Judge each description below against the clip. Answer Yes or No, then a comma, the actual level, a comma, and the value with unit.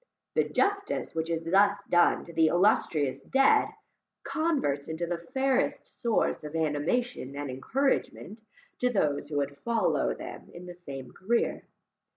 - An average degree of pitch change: No, wide, 8.3 semitones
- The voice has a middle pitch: Yes, medium, 175 Hz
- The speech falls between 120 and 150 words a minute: Yes, average, 145 wpm